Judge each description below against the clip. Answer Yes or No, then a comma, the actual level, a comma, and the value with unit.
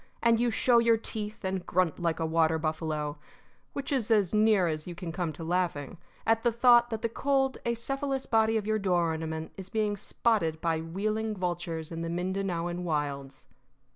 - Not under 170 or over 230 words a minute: Yes, average, 185 wpm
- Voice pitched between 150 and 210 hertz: Yes, medium, 185 Hz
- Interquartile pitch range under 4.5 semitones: No, average, 5.3 semitones